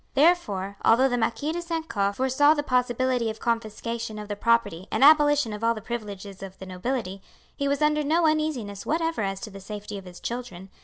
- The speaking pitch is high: Yes, high, 230 Hz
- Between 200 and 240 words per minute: Yes, fast, 205 wpm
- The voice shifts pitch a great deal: Yes, wide, 6.2 semitones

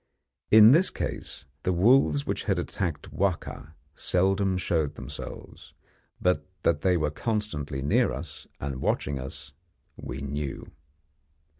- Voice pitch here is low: Yes, very low, 80 Hz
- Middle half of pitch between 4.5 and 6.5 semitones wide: Yes, average, 5.2 semitones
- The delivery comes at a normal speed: No, slow, 125 wpm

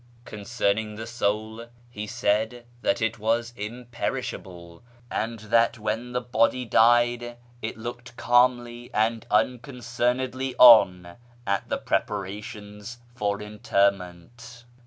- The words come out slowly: Yes, slow, 110 wpm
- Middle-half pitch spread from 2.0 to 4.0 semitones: Yes, narrow, 2.5 semitones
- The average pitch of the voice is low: Yes, low, 115 Hz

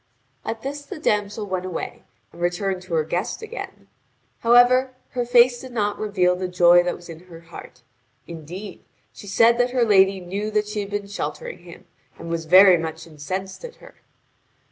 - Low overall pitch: No, high, 200 Hz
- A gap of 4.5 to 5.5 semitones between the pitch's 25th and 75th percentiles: Yes, average, 5.1 semitones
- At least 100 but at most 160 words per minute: No, average, 185 wpm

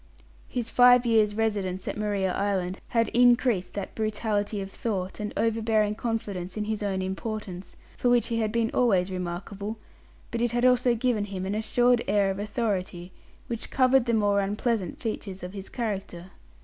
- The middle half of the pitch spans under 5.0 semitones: Yes, average, 3.2 semitones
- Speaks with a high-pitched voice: Yes, high, 210 Hz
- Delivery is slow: No, average, 170 wpm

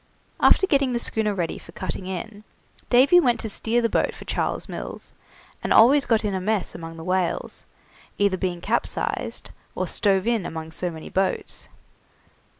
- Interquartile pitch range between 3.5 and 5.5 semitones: Yes, average, 4.5 semitones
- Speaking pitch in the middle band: No, high, 205 Hz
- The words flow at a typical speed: Yes, average, 170 wpm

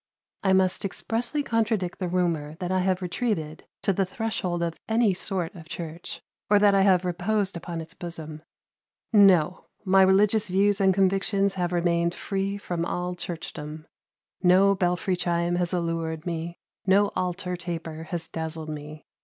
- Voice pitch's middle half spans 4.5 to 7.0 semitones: No, narrow, 2.5 semitones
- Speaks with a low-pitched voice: No, medium, 180 Hz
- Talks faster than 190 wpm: No, average, 155 wpm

